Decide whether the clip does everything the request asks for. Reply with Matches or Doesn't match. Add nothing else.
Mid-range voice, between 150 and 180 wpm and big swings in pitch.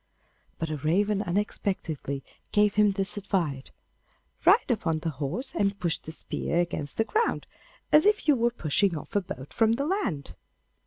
Doesn't match